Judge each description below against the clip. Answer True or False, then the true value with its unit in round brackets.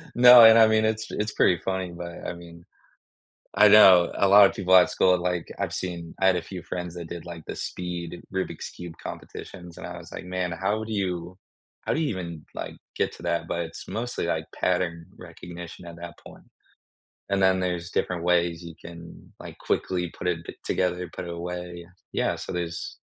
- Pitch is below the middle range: True (90 Hz)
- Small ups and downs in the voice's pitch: True (1.7 semitones)